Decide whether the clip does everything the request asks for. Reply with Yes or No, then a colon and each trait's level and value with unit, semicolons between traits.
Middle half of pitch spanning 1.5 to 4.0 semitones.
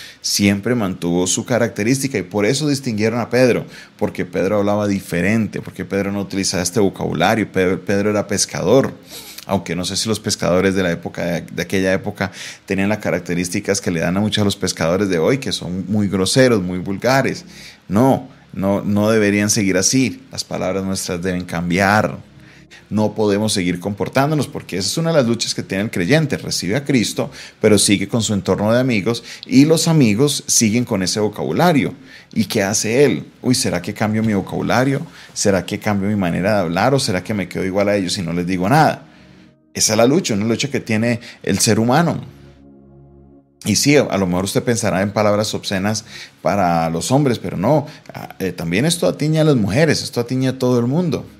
Yes: average, 3.7 semitones